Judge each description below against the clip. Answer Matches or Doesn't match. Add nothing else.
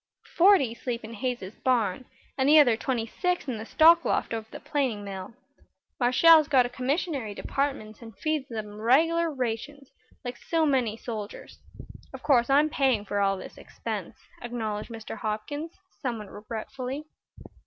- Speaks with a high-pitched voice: Matches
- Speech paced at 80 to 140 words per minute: Doesn't match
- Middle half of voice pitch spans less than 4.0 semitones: Doesn't match